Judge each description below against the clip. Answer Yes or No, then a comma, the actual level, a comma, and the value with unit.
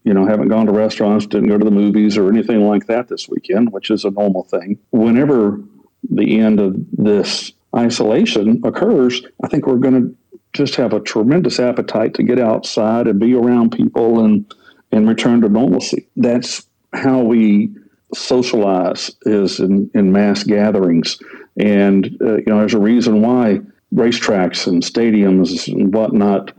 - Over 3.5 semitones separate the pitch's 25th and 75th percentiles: No, narrow, 2.4 semitones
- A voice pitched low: Yes, low, 110 Hz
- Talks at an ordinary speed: Yes, average, 165 wpm